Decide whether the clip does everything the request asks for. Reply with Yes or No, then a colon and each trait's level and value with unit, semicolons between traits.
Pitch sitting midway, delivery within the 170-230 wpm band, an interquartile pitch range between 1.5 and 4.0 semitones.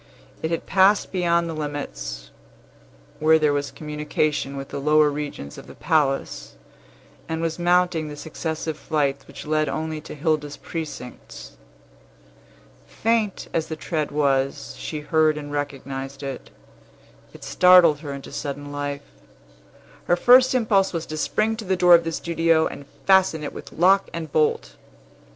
No: medium, 155 Hz; average, 150 wpm; average, 2.9 semitones